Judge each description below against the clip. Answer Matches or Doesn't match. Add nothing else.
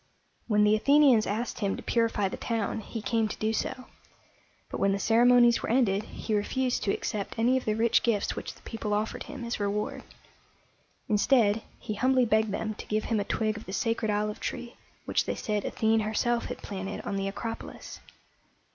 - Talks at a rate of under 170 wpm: Doesn't match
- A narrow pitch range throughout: Matches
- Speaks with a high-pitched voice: Matches